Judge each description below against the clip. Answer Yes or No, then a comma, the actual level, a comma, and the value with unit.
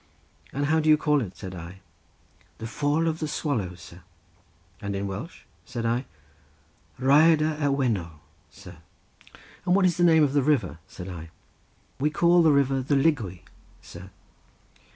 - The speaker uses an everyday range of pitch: No, wide, 8.1 semitones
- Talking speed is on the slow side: No, average, 160 wpm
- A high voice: No, low, 135 Hz